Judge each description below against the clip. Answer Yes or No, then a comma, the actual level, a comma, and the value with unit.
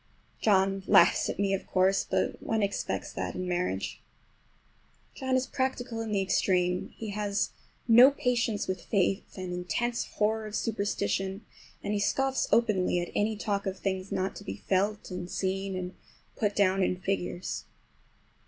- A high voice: Yes, high, 200 Hz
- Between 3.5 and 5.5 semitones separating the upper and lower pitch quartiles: No, average, 2.7 semitones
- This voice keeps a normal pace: Yes, average, 160 wpm